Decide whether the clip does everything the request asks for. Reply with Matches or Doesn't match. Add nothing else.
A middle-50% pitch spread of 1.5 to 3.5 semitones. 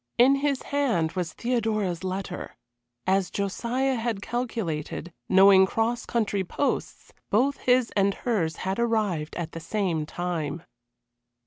Doesn't match